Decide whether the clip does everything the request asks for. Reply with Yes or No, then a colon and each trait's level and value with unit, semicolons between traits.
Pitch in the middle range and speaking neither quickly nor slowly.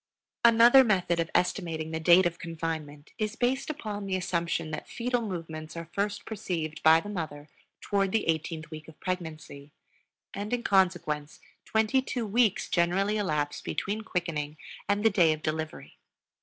Yes: medium, 175 Hz; average, 155 wpm